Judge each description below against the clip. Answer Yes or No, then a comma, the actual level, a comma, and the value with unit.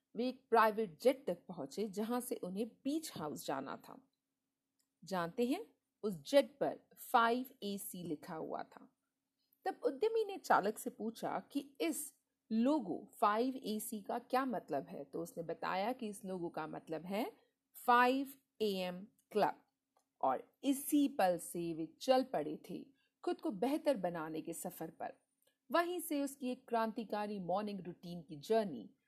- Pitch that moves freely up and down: Yes, wide, 6.5 semitones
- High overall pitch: Yes, high, 230 Hz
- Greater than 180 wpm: No, average, 155 wpm